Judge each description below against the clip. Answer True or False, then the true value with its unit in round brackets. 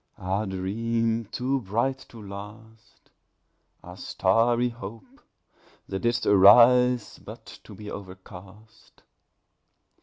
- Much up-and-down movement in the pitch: False (3.2 semitones)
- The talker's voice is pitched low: True (110 Hz)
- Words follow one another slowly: True (95 wpm)